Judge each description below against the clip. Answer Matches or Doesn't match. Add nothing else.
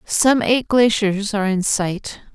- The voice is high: Matches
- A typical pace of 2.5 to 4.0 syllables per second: Matches